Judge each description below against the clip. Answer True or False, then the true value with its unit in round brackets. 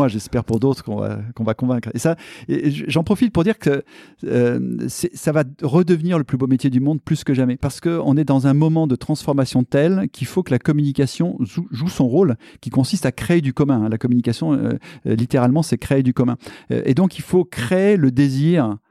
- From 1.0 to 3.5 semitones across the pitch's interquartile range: False (4.7 semitones)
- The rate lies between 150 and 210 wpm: False (220 wpm)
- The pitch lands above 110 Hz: True (140 Hz)